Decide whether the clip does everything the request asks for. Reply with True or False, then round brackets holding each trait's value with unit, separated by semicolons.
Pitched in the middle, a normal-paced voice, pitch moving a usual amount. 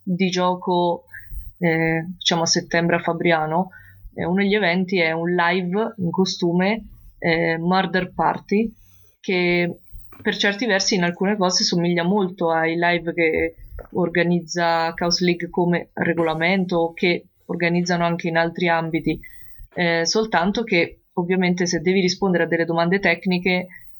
False (175 Hz; 135 wpm; 1.7 semitones)